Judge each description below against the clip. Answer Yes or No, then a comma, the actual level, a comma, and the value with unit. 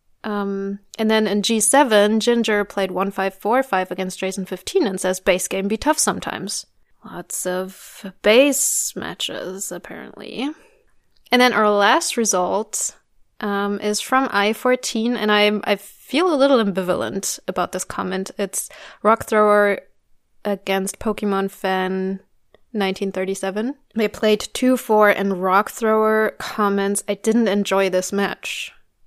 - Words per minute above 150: No, slow, 135 wpm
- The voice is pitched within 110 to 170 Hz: No, high, 205 Hz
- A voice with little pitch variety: Yes, narrow, 2.3 semitones